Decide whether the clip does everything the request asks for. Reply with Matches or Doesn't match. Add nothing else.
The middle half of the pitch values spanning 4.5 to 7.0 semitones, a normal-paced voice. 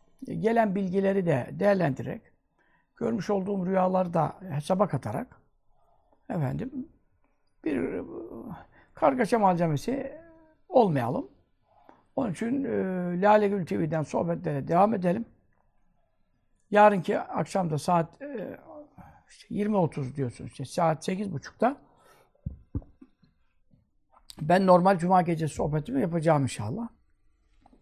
Doesn't match